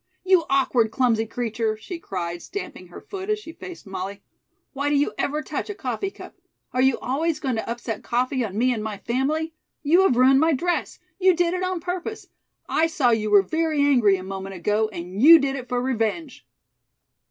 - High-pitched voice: Yes, very high, 260 Hz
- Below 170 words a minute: No, average, 200 wpm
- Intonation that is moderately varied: No, wide, 6.8 semitones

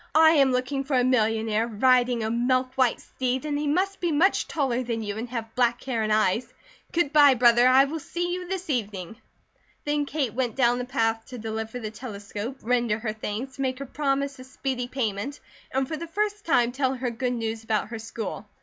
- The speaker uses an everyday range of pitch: Yes, average, 3.6 semitones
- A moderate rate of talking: No, fast, 210 wpm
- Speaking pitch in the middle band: No, very high, 250 Hz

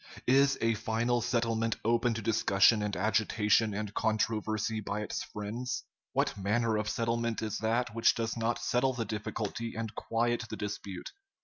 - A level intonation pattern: Yes, narrow, 1.7 semitones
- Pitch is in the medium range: No, low, 115 Hz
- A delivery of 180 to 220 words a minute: No, average, 155 wpm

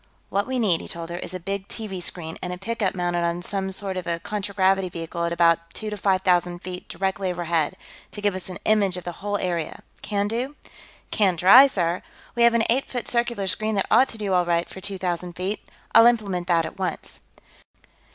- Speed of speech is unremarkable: No, fast, 220 wpm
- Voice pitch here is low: No, high, 190 Hz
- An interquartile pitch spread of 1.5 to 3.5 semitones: Yes, average, 2.9 semitones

